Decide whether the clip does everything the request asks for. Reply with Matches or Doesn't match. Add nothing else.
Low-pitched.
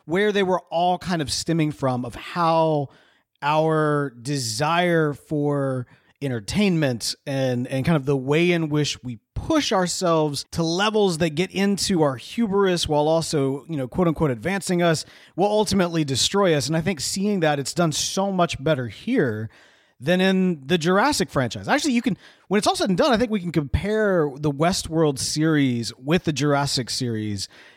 Doesn't match